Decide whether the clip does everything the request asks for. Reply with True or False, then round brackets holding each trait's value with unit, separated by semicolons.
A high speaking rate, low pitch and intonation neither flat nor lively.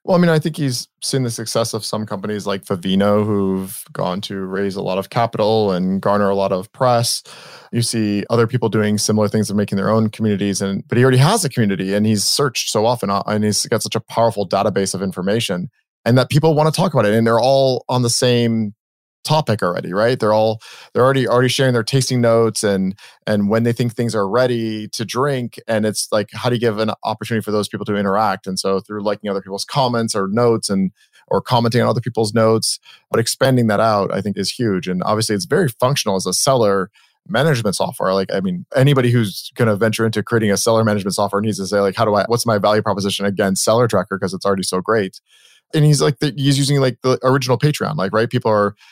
True (235 wpm; 110 Hz; 3.5 semitones)